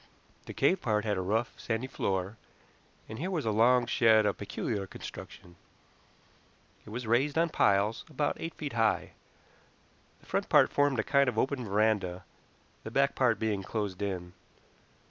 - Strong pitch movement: No, average, 4.2 semitones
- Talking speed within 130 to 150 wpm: No, average, 165 wpm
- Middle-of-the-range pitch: No, low, 110 Hz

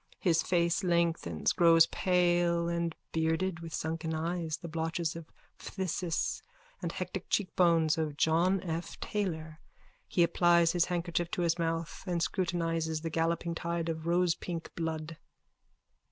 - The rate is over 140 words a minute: No, slow, 135 wpm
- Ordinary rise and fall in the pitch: No, narrow, 1.2 semitones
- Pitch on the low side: No, medium, 170 Hz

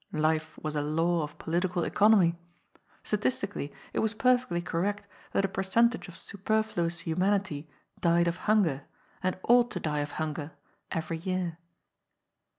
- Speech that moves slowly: No, average, 155 wpm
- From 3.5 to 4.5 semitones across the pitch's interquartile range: Yes, average, 4.1 semitones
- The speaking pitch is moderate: Yes, medium, 175 Hz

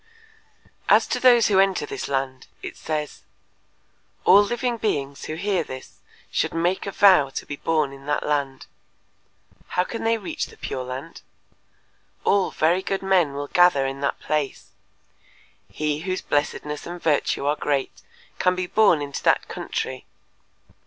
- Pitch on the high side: No, medium, 155 Hz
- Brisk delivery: No, average, 155 wpm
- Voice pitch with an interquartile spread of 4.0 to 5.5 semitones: Yes, average, 5.2 semitones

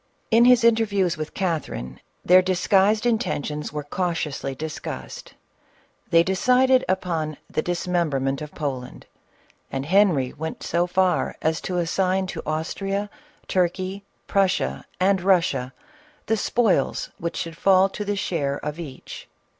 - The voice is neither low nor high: Yes, medium, 180 Hz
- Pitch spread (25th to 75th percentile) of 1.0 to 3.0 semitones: No, average, 4.1 semitones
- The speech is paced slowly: Yes, slow, 130 wpm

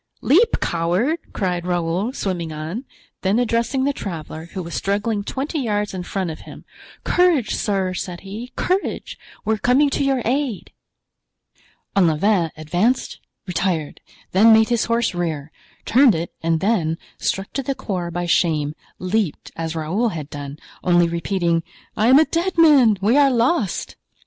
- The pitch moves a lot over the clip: Yes, wide, 6.2 semitones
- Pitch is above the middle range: Yes, high, 195 Hz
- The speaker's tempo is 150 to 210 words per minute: Yes, average, 155 wpm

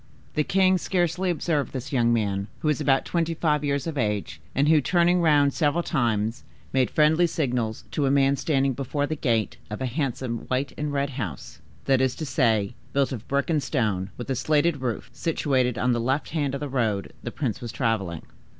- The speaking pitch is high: No, low, 135 Hz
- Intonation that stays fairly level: No, average, 4.2 semitones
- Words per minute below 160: No, fast, 205 wpm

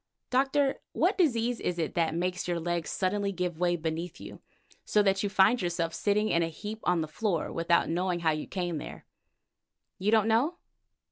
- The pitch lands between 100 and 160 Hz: No, medium, 180 Hz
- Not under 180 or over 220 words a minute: Yes, average, 190 wpm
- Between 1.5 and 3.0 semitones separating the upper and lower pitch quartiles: No, average, 4.2 semitones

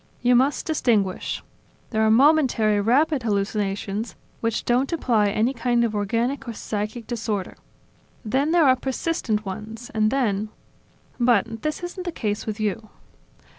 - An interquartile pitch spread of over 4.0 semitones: No, average, 3.7 semitones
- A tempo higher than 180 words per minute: No, average, 140 wpm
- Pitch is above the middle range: Yes, high, 230 Hz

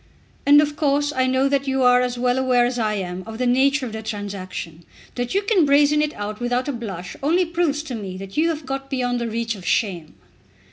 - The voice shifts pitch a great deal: No, average, 4.7 semitones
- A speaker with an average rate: No, fast, 235 wpm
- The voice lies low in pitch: No, very high, 250 Hz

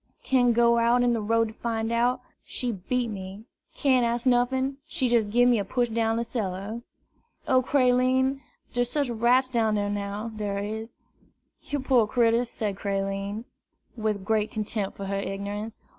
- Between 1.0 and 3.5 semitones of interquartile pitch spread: Yes, average, 2.9 semitones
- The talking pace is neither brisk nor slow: Yes, average, 165 wpm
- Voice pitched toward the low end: No, high, 230 Hz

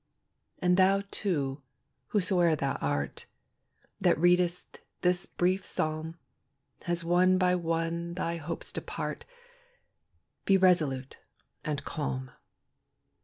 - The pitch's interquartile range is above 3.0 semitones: No, average, 2.7 semitones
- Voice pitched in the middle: Yes, medium, 170 Hz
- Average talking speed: No, slow, 100 wpm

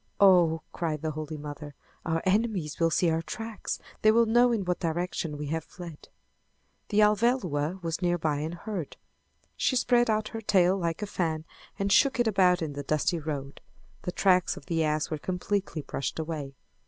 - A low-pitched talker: No, medium, 175 Hz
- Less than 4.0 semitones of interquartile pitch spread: No, average, 4.5 semitones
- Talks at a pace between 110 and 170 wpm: No, average, 180 wpm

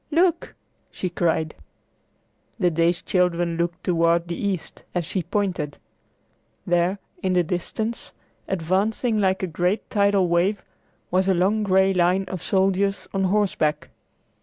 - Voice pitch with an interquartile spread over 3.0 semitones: No, narrow, 2.5 semitones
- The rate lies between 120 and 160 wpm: Yes, slow, 135 wpm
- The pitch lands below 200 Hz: Yes, medium, 185 Hz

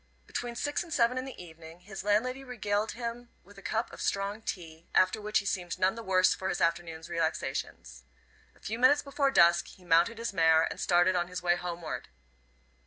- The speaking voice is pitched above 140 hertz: Yes, high, 190 Hz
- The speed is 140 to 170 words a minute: No, average, 200 wpm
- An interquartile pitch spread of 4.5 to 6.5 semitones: Yes, average, 5.1 semitones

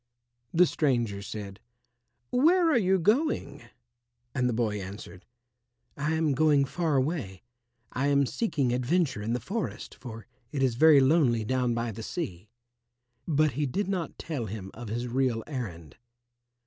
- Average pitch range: No, wide, 5.8 semitones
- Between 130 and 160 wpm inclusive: Yes, average, 150 wpm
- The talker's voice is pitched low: Yes, low, 130 Hz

